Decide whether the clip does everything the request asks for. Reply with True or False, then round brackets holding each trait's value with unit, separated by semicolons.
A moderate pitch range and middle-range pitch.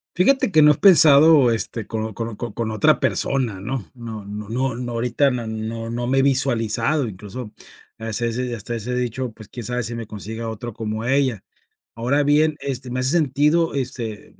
False (3.4 semitones; 120 Hz)